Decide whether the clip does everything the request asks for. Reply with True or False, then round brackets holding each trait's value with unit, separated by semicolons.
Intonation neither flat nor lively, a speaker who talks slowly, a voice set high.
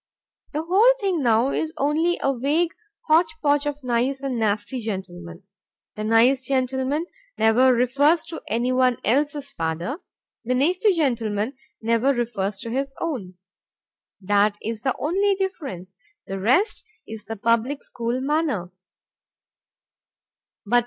True (5.0 semitones; 125 wpm; 255 Hz)